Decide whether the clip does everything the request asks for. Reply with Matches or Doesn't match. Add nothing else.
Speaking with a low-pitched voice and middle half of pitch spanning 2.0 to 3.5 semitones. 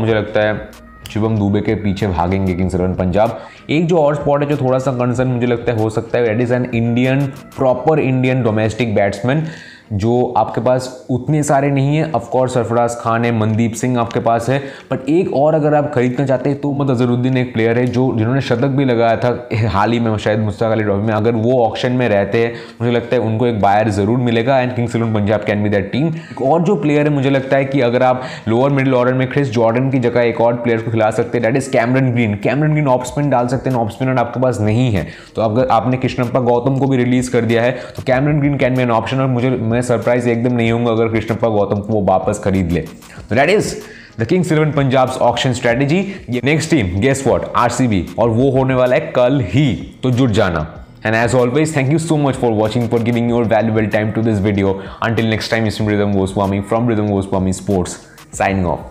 Matches